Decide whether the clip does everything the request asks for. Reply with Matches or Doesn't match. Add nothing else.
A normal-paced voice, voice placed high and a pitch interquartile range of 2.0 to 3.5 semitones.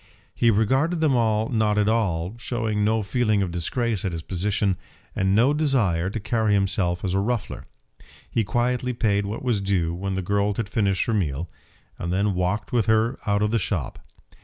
Doesn't match